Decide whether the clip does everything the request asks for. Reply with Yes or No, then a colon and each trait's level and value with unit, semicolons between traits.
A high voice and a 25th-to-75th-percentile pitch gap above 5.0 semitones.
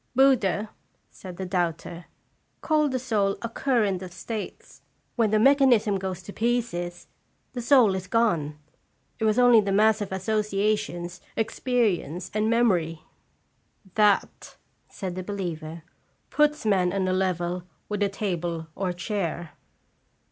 No: high, 200 Hz; average, 3.9 semitones